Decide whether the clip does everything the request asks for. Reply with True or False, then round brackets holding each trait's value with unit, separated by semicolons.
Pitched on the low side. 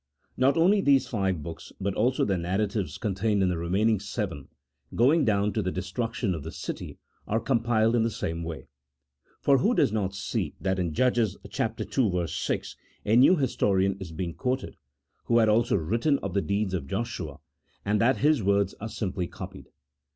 True (105 Hz)